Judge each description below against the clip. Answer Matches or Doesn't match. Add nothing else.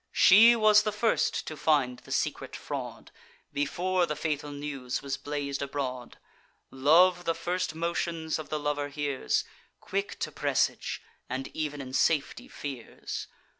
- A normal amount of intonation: Matches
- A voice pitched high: Doesn't match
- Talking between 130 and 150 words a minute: Matches